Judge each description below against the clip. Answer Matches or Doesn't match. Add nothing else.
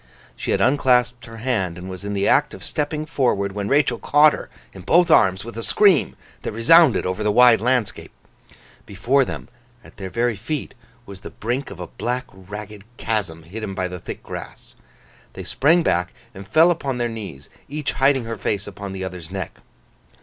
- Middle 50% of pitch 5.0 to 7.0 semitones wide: Matches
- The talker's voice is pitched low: Matches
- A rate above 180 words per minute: Matches